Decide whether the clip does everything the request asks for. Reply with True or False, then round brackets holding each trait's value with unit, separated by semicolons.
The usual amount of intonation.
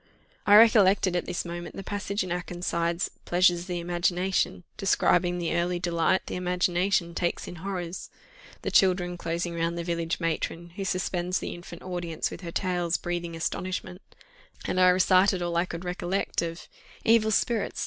False (1.4 semitones)